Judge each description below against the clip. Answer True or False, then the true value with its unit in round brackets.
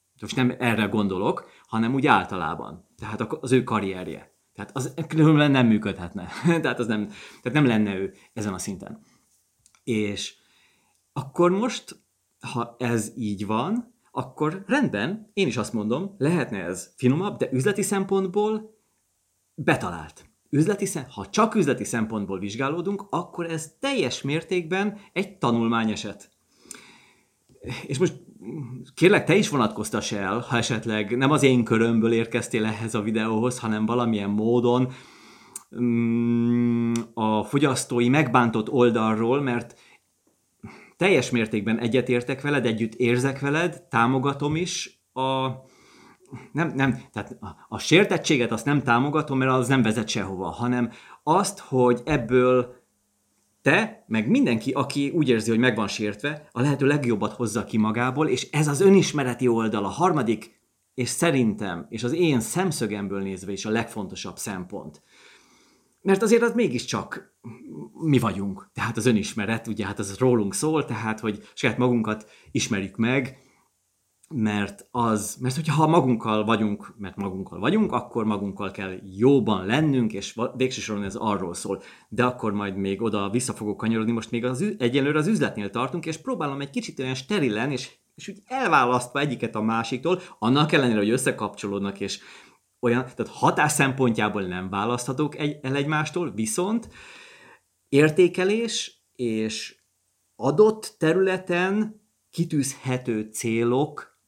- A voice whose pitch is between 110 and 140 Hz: True (125 Hz)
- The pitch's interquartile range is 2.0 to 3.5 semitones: False (5.4 semitones)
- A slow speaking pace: False (135 wpm)